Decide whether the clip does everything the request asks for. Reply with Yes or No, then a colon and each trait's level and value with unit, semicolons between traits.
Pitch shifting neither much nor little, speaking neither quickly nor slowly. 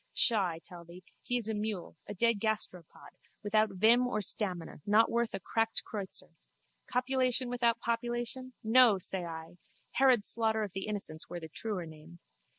Yes: average, 4.5 semitones; average, 165 wpm